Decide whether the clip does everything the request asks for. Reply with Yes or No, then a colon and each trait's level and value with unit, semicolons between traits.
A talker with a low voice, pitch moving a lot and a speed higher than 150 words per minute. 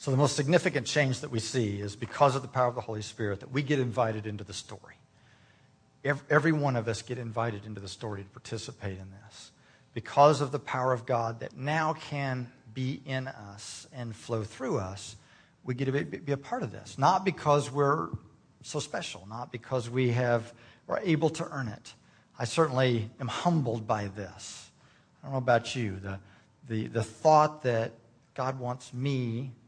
No: low, 125 Hz; average, 4.1 semitones; average, 190 wpm